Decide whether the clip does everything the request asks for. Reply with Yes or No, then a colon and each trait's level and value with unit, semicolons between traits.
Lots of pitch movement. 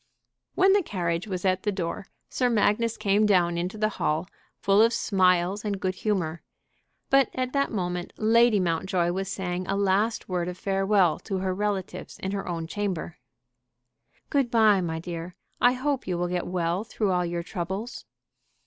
No: average, 3.3 semitones